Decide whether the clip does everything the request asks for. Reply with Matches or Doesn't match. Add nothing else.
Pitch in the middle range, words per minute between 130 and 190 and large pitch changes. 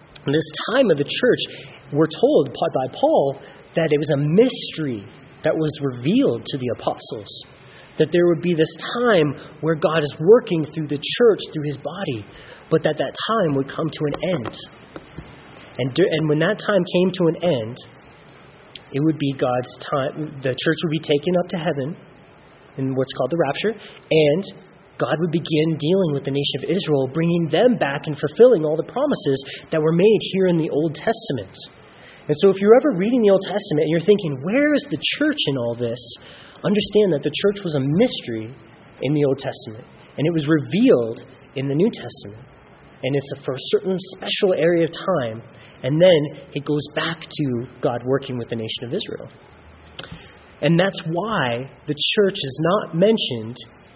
Doesn't match